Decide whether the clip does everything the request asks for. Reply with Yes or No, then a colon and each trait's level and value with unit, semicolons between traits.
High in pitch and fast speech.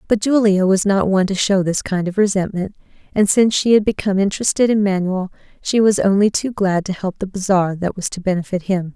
Yes: high, 195 Hz; fast, 220 wpm